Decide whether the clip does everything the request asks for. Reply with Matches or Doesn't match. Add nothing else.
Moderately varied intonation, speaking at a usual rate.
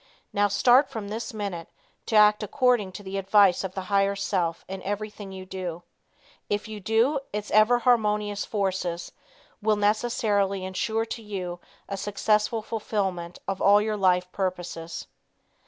Doesn't match